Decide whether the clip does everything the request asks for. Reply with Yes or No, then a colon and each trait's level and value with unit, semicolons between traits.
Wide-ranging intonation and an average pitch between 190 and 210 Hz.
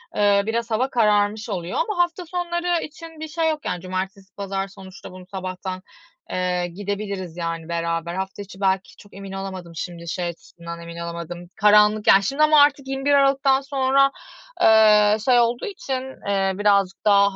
Yes: wide, 6.2 semitones; high, 200 Hz